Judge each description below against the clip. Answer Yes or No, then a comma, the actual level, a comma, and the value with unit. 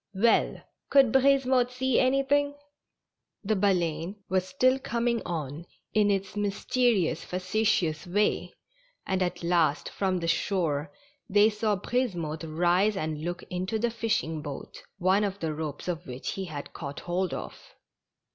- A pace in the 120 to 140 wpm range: Yes, slow, 135 wpm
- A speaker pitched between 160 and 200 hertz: Yes, high, 190 Hz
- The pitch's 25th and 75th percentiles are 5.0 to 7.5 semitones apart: Yes, average, 5.3 semitones